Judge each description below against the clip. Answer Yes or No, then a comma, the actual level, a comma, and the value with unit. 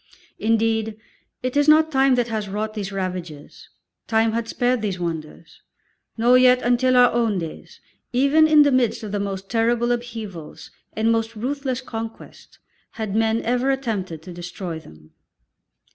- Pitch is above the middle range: Yes, high, 225 Hz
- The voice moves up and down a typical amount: Yes, average, 4.1 semitones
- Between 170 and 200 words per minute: No, average, 155 wpm